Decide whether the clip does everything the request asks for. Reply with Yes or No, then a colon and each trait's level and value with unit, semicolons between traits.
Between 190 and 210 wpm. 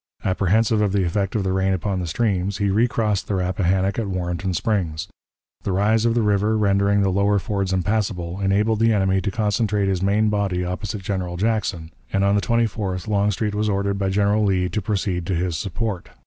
Yes: average, 195 wpm